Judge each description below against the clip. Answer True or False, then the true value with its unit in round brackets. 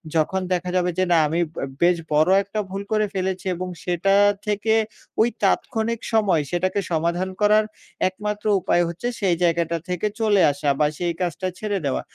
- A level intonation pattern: False (3.4 semitones)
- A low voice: False (185 Hz)